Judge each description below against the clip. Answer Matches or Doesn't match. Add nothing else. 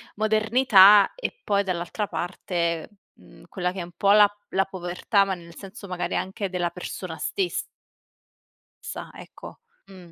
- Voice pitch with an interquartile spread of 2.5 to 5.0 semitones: Matches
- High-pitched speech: Matches